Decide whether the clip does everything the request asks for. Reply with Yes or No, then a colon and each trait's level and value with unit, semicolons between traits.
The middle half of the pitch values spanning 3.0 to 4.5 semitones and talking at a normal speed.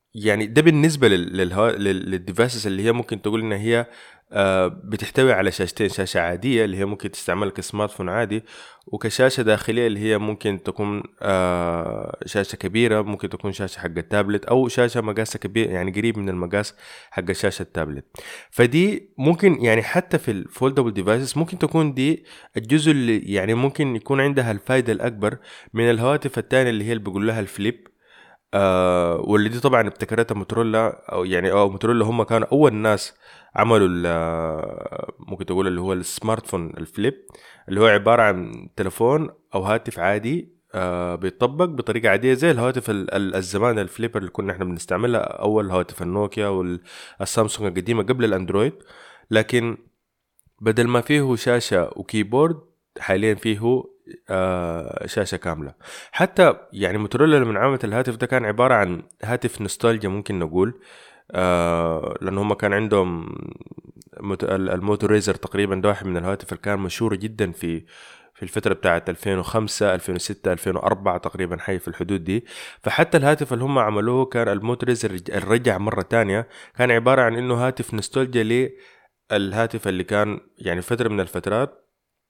No: average, 4.0 semitones; fast, 145 wpm